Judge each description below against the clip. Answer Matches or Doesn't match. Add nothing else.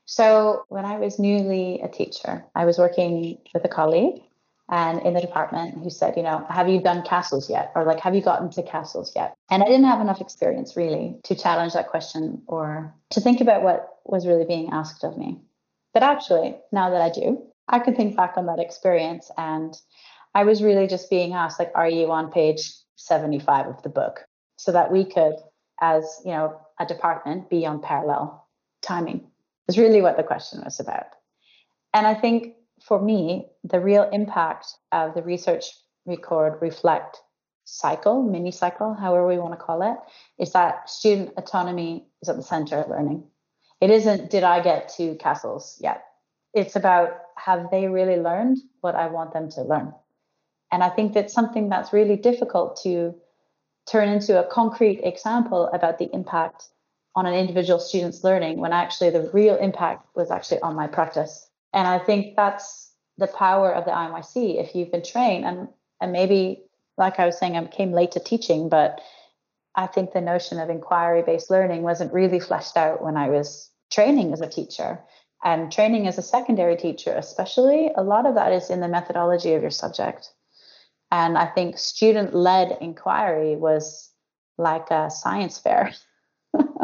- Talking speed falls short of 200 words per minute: Matches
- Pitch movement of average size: Matches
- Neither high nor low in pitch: Matches